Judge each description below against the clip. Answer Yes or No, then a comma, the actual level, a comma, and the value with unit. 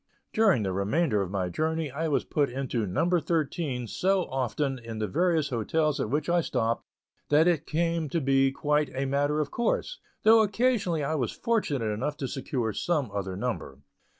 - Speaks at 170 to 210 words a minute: Yes, average, 180 wpm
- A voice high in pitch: No, medium, 145 Hz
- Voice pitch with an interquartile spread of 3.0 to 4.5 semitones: No, average, 5.3 semitones